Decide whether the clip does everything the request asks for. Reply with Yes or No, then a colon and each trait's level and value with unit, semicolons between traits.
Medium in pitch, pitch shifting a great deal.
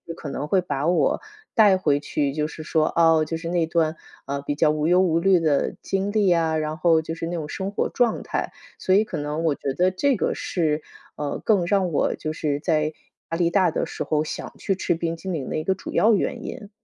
No: medium, 165 Hz; average, 3.4 semitones